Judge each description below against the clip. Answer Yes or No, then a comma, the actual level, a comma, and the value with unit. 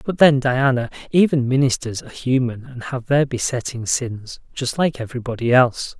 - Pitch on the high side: No, low, 130 Hz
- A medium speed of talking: Yes, average, 160 wpm